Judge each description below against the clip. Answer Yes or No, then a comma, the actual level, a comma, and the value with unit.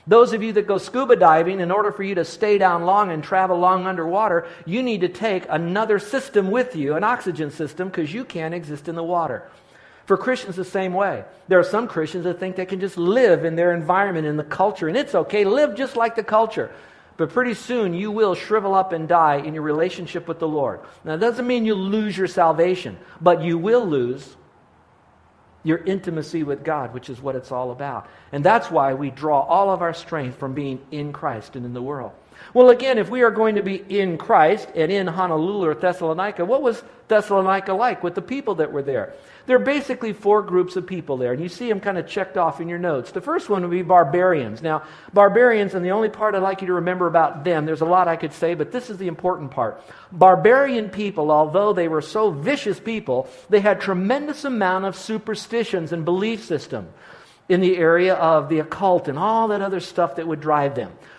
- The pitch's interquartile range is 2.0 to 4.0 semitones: No, average, 4.5 semitones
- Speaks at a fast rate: Yes, fast, 225 wpm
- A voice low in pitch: No, medium, 185 Hz